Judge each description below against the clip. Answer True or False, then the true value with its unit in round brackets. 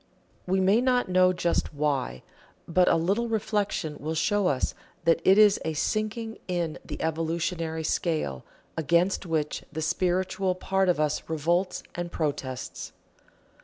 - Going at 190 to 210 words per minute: False (140 wpm)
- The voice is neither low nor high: True (175 Hz)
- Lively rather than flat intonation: False (3.3 semitones)